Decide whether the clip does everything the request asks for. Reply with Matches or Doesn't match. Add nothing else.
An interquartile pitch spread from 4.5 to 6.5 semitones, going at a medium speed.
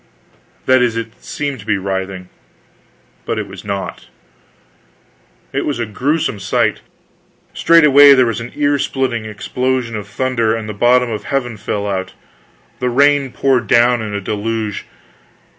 Doesn't match